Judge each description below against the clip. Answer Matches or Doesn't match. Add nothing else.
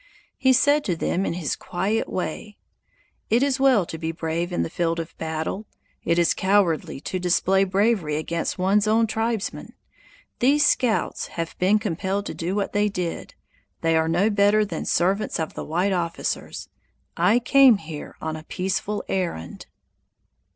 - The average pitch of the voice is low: Doesn't match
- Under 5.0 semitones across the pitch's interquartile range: Matches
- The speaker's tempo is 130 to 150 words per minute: Doesn't match